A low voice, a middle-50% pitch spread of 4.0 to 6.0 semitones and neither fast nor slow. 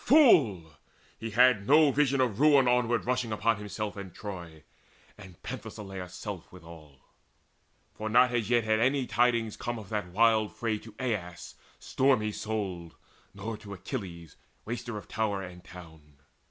Yes: low, 110 Hz; average, 4.5 semitones; average, 150 wpm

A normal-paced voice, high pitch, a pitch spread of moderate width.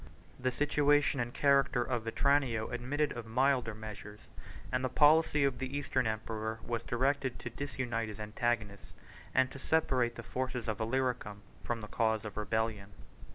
No: average, 155 wpm; low, 120 Hz; average, 3.4 semitones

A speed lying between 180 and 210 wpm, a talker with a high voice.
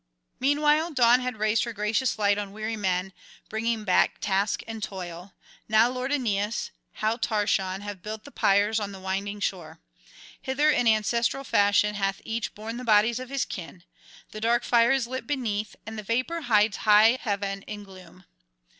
No: average, 170 wpm; high, 215 Hz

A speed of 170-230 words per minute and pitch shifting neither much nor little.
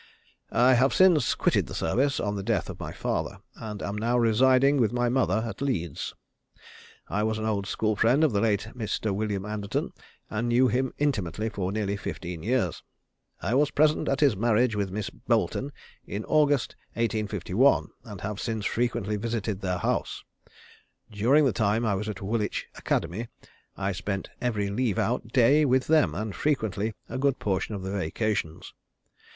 Yes: average, 175 wpm; average, 3.8 semitones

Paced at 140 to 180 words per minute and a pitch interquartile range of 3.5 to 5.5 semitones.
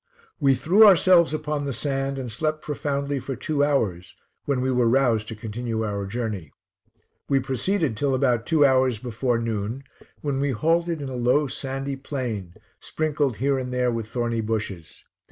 Yes: average, 170 wpm; average, 3.9 semitones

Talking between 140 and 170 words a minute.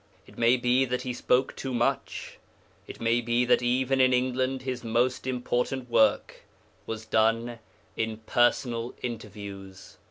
Yes: average, 145 wpm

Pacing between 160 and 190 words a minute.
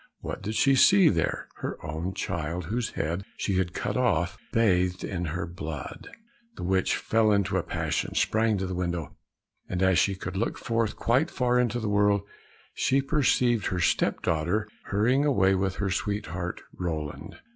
Yes: average, 170 wpm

